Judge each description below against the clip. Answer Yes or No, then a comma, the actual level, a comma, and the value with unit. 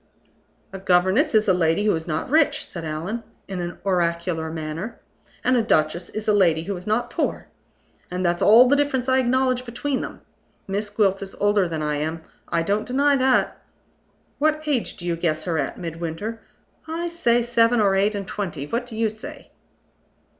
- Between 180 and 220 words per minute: Yes, average, 190 wpm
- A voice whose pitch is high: Yes, high, 205 Hz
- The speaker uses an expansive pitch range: Yes, wide, 6.2 semitones